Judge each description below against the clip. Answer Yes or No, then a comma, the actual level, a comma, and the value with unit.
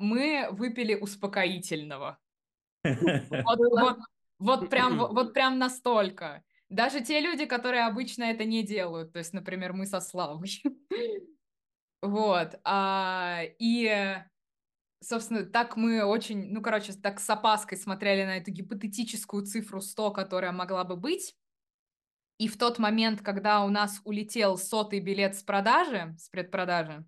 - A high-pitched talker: Yes, high, 210 Hz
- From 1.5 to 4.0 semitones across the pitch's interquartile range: Yes, average, 3.7 semitones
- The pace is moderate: Yes, average, 135 wpm